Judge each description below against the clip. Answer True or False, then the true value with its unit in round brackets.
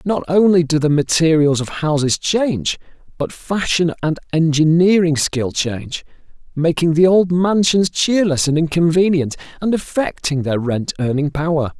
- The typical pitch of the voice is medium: True (160 Hz)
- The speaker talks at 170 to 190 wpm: False (135 wpm)